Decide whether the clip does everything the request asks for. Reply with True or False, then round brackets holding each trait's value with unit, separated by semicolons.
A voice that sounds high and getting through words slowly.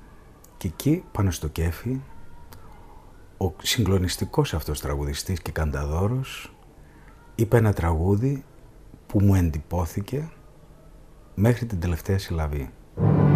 False (95 Hz; 95 wpm)